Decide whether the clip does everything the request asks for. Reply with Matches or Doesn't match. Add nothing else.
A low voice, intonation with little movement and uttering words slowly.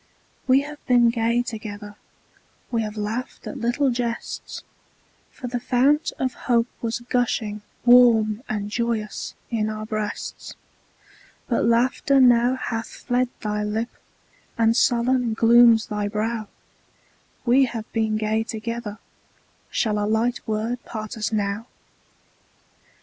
Doesn't match